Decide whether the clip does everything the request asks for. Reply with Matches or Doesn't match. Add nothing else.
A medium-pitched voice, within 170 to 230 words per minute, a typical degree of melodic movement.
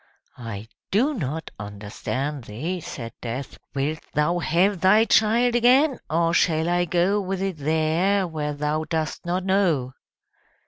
Doesn't match